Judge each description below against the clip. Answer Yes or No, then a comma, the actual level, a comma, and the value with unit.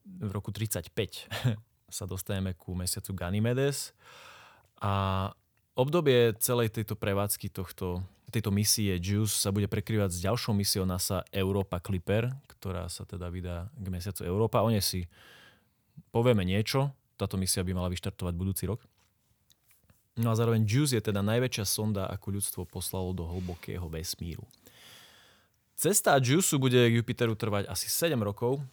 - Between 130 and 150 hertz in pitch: No, low, 100 Hz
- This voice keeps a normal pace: Yes, average, 140 wpm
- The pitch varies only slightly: No, average, 3.4 semitones